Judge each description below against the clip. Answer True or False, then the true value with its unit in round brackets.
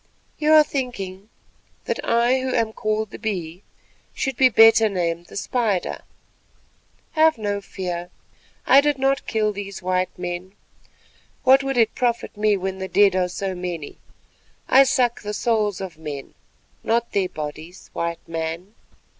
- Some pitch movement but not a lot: True (4.9 semitones)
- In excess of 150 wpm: False (145 wpm)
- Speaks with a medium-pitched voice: False (205 Hz)